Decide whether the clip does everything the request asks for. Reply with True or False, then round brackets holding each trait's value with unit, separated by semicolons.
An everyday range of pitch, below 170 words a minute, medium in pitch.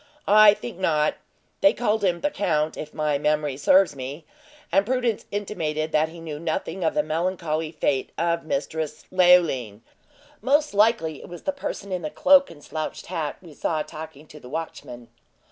False (4.0 semitones; 175 wpm; 160 Hz)